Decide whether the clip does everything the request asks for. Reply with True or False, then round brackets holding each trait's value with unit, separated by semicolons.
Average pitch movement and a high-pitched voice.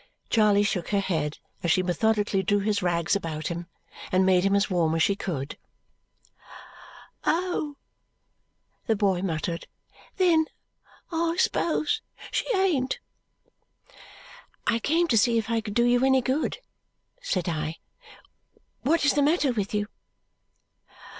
False (6.9 semitones; 205 Hz)